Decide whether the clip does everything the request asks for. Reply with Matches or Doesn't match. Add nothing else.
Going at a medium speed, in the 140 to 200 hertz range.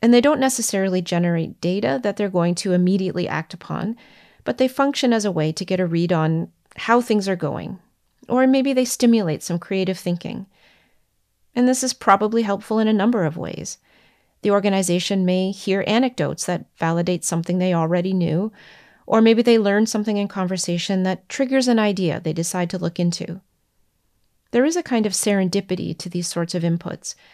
Matches